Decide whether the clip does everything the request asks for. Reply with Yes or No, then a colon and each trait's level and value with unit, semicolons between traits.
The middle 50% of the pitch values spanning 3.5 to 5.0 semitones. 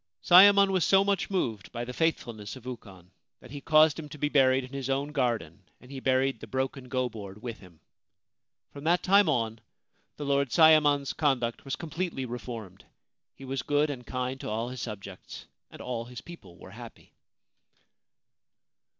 Yes: average, 4.1 semitones